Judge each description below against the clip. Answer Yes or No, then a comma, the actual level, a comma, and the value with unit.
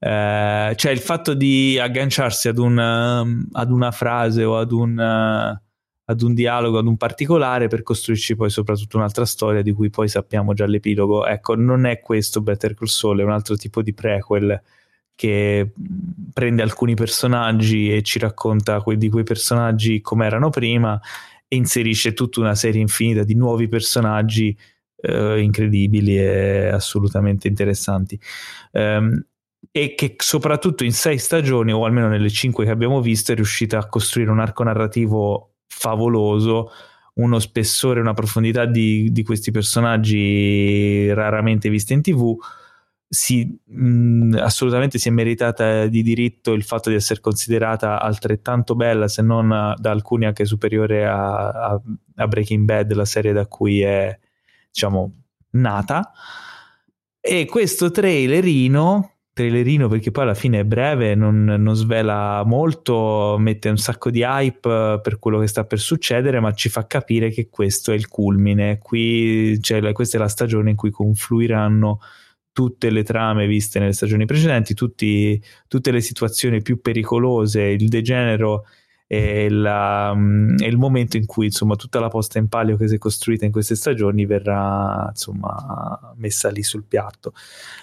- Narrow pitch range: Yes, narrow, 2.1 semitones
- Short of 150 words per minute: No, average, 155 wpm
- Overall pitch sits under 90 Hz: No, low, 110 Hz